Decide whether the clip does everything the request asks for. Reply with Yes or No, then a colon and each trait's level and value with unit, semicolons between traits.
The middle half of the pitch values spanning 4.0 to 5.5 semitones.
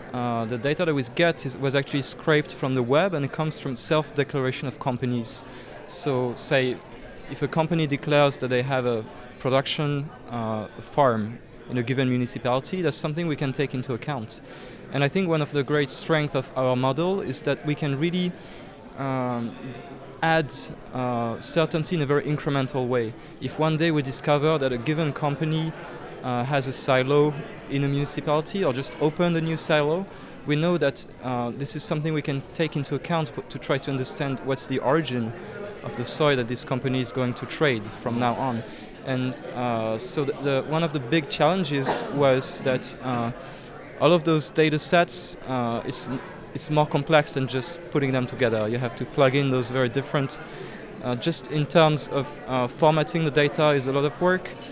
No: average, 3.3 semitones